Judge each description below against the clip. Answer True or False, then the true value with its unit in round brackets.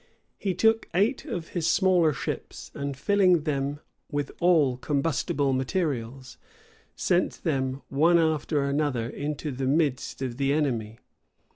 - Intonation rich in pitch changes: False (3.9 semitones)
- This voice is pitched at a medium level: True (145 Hz)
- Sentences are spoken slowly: True (130 wpm)